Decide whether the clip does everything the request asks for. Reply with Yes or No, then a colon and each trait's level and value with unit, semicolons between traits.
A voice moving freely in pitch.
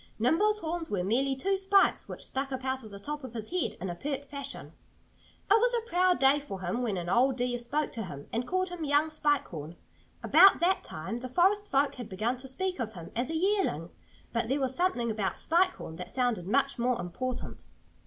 Yes: wide, 6.8 semitones